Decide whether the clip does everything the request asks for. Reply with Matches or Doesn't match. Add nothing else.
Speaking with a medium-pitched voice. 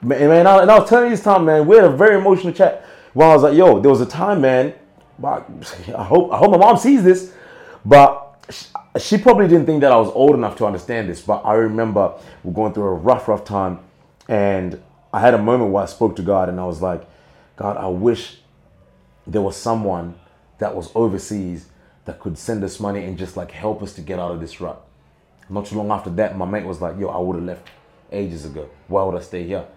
Doesn't match